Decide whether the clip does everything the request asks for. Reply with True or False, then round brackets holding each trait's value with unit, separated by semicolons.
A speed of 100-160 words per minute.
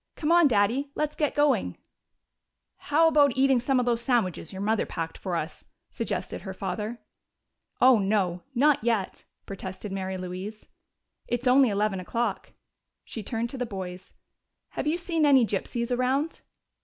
True (155 wpm)